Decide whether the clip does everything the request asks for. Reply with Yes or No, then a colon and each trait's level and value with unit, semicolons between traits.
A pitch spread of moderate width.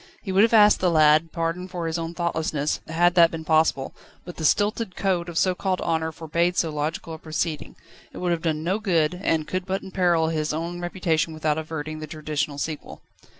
No: narrow, 2.3 semitones